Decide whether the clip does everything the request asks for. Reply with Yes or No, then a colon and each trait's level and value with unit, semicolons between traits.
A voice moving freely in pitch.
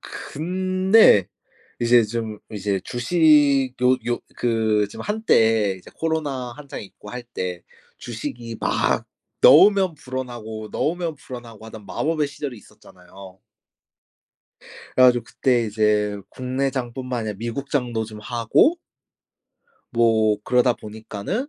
No: average, 4.2 semitones